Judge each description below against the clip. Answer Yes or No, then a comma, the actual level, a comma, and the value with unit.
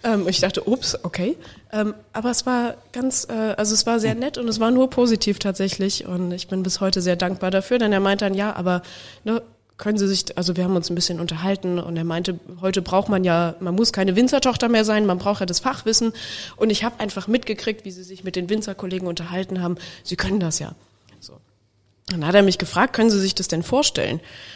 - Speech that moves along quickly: Yes, fast, 220 wpm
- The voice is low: No, high, 195 Hz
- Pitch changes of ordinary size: Yes, average, 3.4 semitones